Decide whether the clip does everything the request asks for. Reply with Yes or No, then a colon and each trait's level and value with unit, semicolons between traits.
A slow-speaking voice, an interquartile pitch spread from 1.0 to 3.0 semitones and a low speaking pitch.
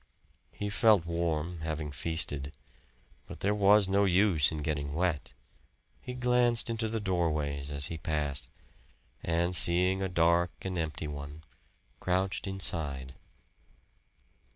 No: slow, 125 wpm; average, 4.2 semitones; very low, 85 Hz